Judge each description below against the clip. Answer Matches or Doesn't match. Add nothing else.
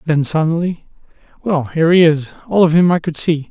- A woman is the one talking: Doesn't match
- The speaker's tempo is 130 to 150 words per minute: Doesn't match